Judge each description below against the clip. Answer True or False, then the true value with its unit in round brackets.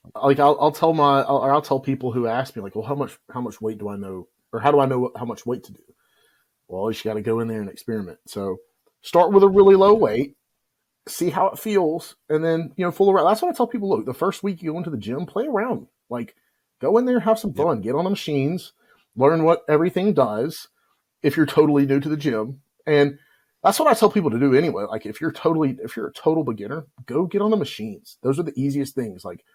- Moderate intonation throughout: False (6.4 semitones)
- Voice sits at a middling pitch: True (150 Hz)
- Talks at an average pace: False (260 wpm)